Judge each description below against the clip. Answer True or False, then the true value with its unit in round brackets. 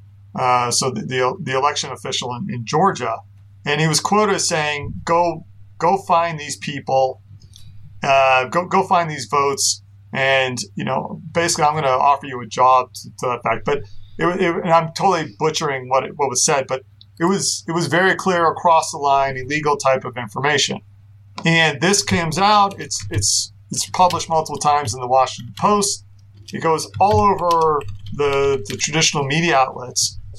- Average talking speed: True (180 wpm)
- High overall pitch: False (140 Hz)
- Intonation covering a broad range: True (6.4 semitones)